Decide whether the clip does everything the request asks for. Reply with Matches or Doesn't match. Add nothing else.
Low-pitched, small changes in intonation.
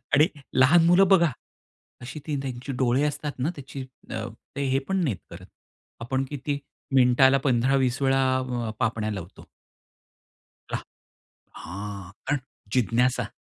Doesn't match